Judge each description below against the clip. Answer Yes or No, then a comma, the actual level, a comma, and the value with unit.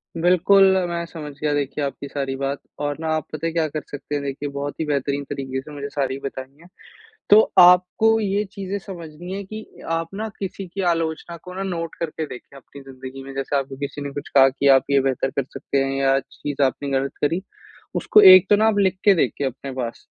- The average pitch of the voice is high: No, medium, 145 Hz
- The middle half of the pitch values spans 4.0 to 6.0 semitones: Yes, average, 4.4 semitones